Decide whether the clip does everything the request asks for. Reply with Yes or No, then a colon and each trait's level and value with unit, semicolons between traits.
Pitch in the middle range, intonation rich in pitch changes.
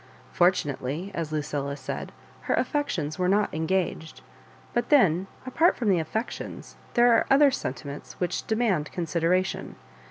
Yes: medium, 180 Hz; wide, 6.3 semitones